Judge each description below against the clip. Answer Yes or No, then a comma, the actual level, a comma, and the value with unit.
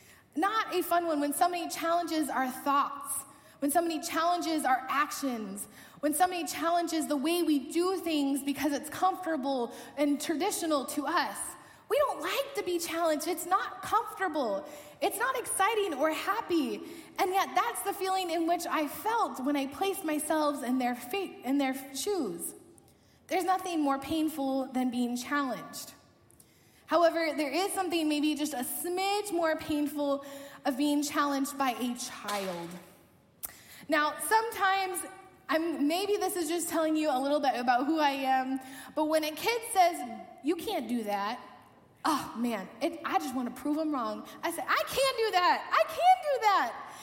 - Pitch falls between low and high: No, very high, 315 Hz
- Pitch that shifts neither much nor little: Yes, average, 4.5 semitones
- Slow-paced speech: No, average, 165 wpm